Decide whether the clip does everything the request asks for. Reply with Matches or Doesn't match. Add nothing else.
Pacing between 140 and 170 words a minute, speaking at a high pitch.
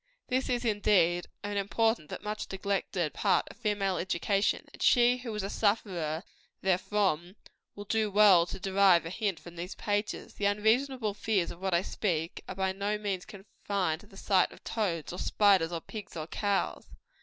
Doesn't match